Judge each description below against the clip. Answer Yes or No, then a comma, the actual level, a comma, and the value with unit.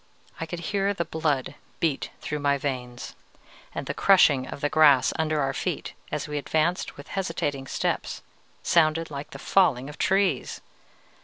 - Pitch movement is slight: No, average, 3.0 semitones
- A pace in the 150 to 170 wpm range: Yes, average, 160 wpm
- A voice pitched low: No, medium, 150 Hz